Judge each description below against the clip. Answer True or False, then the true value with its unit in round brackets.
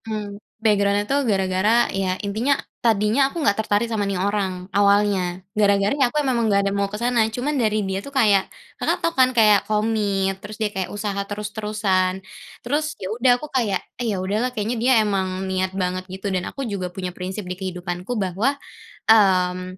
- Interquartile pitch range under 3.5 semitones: True (2.6 semitones)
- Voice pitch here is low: False (205 Hz)